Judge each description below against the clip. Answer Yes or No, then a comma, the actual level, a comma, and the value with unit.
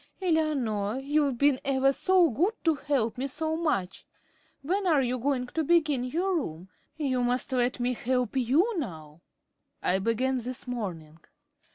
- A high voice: Yes, very high, 260 Hz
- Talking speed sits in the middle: Yes, average, 155 wpm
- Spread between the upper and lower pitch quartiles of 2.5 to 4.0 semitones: No, average, 4.4 semitones